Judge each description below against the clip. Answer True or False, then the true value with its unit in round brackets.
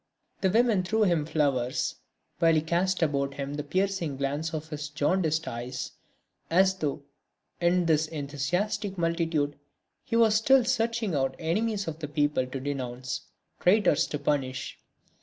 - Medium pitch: True (160 Hz)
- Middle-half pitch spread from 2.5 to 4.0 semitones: False (4.7 semitones)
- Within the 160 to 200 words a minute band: False (145 wpm)